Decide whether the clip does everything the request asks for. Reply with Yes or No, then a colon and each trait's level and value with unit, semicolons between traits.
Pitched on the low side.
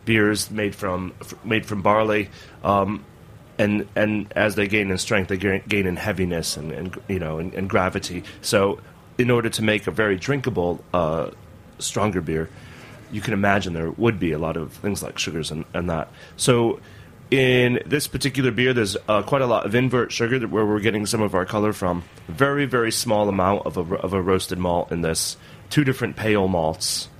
Yes: low, 105 Hz